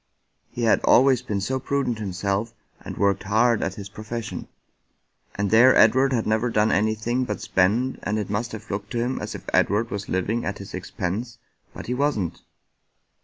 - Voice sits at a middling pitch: No, low, 110 Hz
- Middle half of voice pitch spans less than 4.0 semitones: Yes, average, 3.1 semitones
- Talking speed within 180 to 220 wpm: Yes, average, 185 wpm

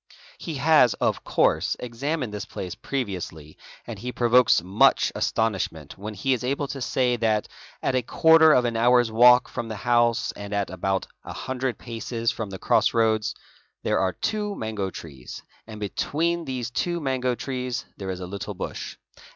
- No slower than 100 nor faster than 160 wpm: No, average, 170 wpm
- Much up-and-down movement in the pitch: No, average, 4.0 semitones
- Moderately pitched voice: No, low, 115 Hz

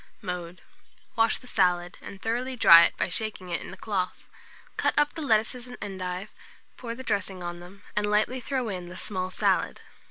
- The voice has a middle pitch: No, high, 200 Hz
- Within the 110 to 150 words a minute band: No, average, 190 wpm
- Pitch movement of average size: Yes, average, 4.3 semitones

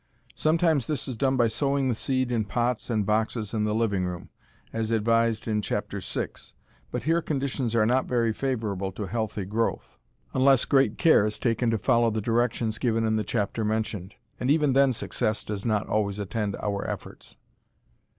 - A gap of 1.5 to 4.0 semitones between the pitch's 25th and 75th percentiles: Yes, average, 3.2 semitones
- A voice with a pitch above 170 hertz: No, low, 115 Hz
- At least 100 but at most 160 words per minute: No, average, 180 wpm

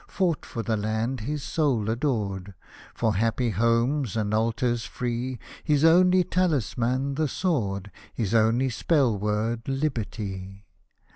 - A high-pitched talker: No, low, 115 Hz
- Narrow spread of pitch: No, average, 4.4 semitones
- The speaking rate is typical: No, slow, 125 wpm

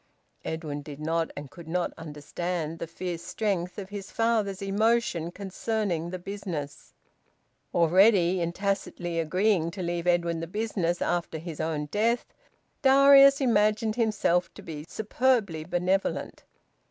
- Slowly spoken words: Yes, slow, 130 wpm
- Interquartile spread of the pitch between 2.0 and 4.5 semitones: Yes, average, 4.0 semitones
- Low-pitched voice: No, medium, 180 Hz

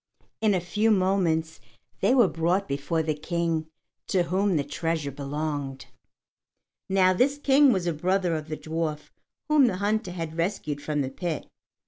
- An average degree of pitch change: Yes, average, 3.9 semitones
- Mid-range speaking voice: Yes, medium, 170 Hz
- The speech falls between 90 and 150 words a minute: No, average, 160 wpm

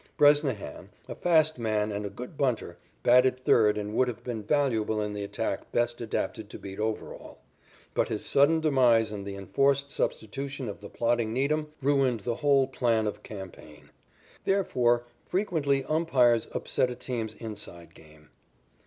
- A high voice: No, low, 120 Hz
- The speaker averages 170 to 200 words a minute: No, average, 155 wpm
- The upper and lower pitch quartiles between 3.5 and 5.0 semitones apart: Yes, average, 4.5 semitones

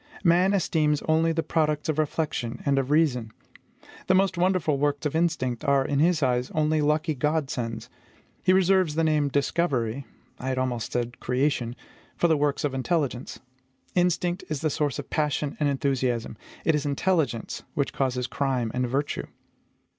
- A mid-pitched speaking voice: Yes, medium, 145 Hz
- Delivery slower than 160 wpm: No, average, 165 wpm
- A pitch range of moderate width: Yes, average, 3.7 semitones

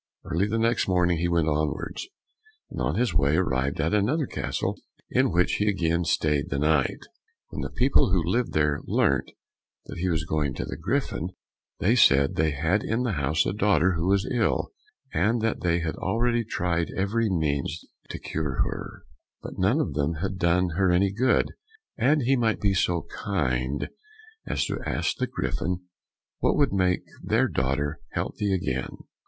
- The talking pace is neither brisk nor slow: Yes, average, 175 wpm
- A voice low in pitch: Yes, very low, 90 Hz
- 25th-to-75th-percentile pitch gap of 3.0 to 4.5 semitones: No, average, 5.1 semitones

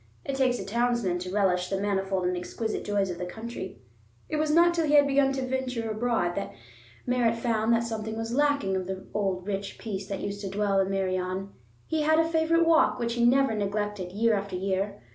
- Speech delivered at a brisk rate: Yes, fast, 210 wpm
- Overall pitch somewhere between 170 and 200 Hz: No, high, 215 Hz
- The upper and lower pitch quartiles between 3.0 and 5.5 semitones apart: Yes, average, 4.5 semitones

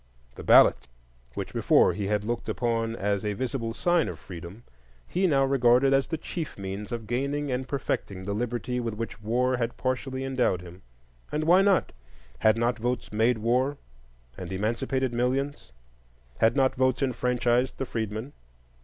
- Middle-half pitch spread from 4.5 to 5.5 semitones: No, average, 3.4 semitones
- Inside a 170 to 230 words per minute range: No, average, 160 wpm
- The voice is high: No, low, 120 Hz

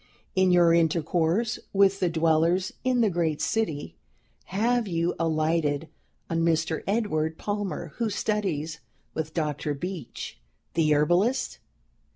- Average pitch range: Yes, average, 3.8 semitones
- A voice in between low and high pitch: Yes, medium, 170 Hz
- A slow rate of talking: Yes, slow, 120 wpm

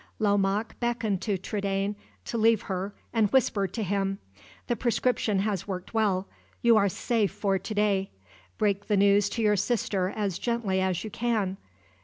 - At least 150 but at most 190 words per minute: Yes, average, 165 wpm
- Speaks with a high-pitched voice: Yes, high, 205 Hz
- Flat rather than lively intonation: Yes, narrow, 2.3 semitones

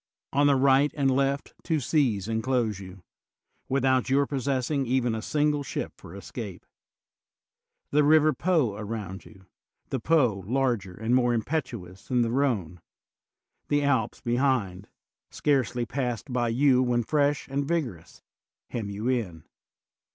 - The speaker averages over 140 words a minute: No, slow, 135 wpm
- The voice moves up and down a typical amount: Yes, average, 4.3 semitones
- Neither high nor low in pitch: No, low, 125 Hz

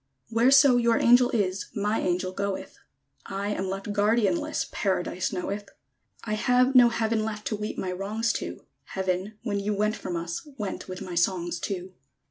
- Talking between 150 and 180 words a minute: Yes, average, 170 wpm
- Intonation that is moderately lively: Yes, average, 3.4 semitones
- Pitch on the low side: No, high, 205 Hz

